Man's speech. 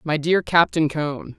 Yes: male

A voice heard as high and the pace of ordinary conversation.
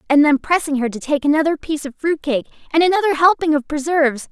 No: very high, 300 Hz; fast, 225 wpm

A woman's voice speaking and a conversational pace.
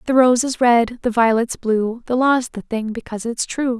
No: female; fast, 220 wpm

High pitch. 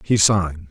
No: very low, 90 Hz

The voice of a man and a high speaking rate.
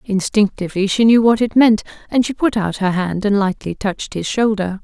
No: female; fast, 210 wpm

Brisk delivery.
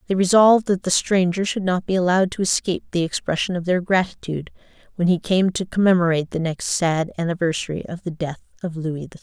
Yes: fast, 210 wpm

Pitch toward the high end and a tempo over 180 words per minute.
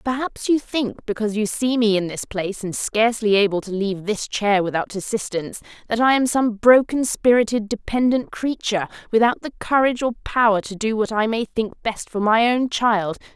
Yes: high, 220 Hz; average, 195 wpm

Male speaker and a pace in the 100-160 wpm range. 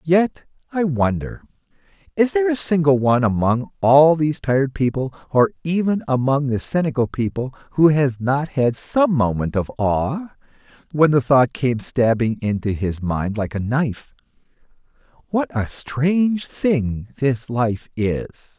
Yes: male; average, 145 wpm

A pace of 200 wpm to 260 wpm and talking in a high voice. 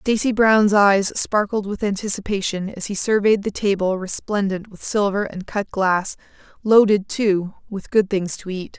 No: average, 155 wpm; high, 200 Hz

